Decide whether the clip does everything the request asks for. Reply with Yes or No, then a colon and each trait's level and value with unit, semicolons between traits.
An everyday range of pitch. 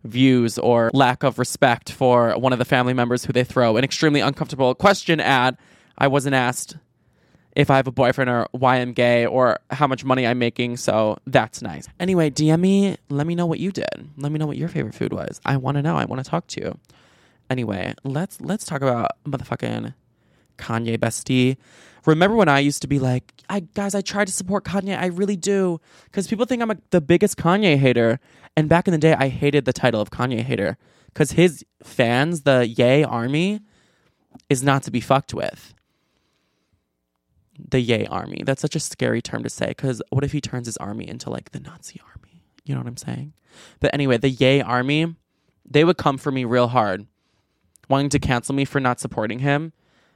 Yes: average, 4.2 semitones